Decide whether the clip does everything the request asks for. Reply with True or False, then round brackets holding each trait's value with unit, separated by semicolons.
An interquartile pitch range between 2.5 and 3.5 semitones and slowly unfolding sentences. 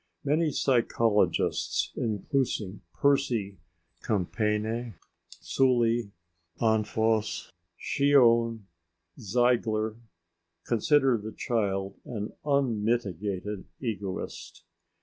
True (2.8 semitones; 60 wpm)